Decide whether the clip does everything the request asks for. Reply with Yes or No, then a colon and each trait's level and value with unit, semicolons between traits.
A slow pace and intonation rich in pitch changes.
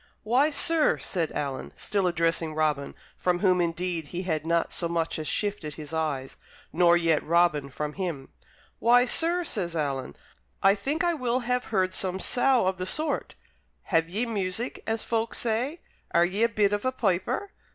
No: average, 175 wpm; wide, 6.0 semitones